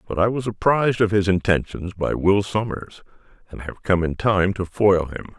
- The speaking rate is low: No, average, 200 wpm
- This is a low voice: Yes, low, 100 Hz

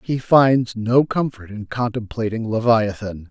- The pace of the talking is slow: Yes, slow, 125 wpm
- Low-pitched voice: Yes, low, 115 Hz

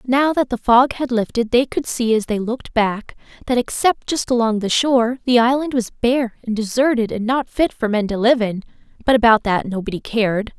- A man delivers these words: No, female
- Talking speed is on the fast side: Yes, fast, 215 wpm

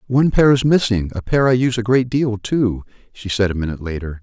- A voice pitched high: No, low, 110 Hz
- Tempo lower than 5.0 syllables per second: No, 6.1 syllables/s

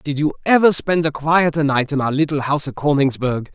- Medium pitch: Yes, medium, 150 Hz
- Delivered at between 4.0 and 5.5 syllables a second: No, 5.7 syllables/s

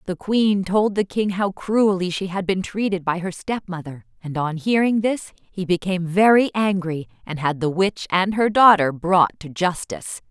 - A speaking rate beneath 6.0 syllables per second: Yes, 4.7 syllables/s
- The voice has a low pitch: No, high, 190 Hz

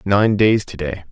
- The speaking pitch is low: Yes, very low, 95 Hz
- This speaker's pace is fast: Yes, fast, 215 wpm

